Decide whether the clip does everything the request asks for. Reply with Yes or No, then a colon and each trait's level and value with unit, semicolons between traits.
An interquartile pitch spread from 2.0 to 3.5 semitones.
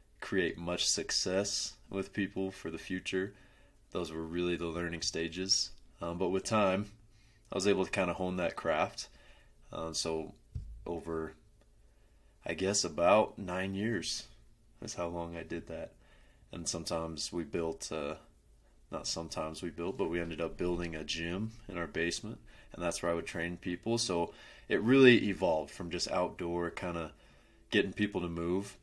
Yes: average, 3.1 semitones